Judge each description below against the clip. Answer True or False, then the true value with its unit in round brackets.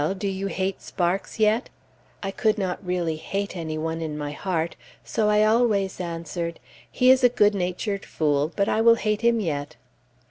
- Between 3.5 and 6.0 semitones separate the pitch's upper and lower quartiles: True (4.3 semitones)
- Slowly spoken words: False (180 wpm)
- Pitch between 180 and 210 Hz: True (190 Hz)